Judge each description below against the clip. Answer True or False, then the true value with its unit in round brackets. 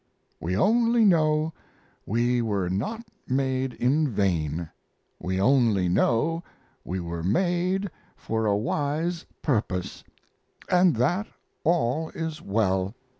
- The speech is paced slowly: True (110 wpm)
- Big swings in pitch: True (8.8 semitones)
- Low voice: True (125 Hz)